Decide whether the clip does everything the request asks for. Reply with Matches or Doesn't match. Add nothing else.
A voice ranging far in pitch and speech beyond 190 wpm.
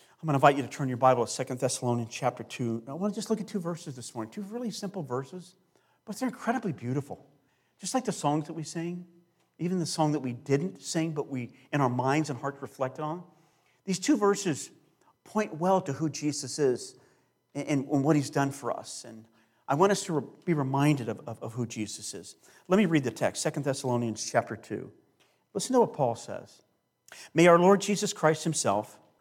Matches